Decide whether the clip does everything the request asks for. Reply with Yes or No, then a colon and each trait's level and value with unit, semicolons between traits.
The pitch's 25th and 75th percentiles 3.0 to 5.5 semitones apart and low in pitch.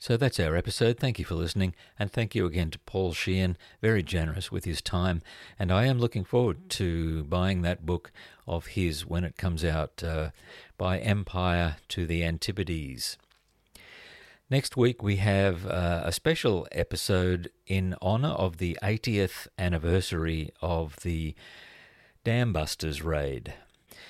Yes: average, 3.3 semitones; very low, 90 Hz